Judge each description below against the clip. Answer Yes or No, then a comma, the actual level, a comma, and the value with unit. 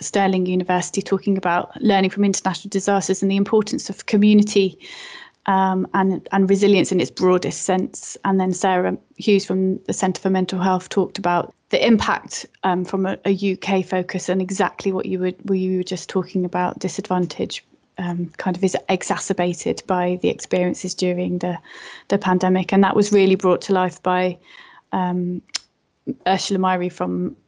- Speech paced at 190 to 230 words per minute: No, average, 170 wpm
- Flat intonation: Yes, narrow, 1.3 semitones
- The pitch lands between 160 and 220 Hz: Yes, medium, 185 Hz